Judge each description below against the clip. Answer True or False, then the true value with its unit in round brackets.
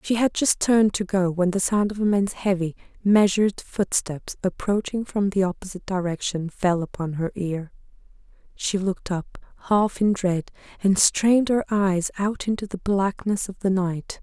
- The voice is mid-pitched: False (195 Hz)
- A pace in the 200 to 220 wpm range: False (175 wpm)